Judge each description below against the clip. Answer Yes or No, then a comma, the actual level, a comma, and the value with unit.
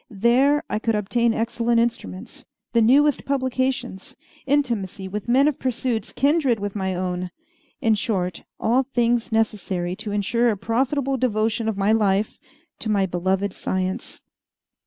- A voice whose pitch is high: Yes, high, 225 Hz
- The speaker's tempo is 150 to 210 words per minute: No, average, 140 wpm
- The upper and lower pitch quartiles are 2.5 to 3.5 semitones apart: No, average, 4.1 semitones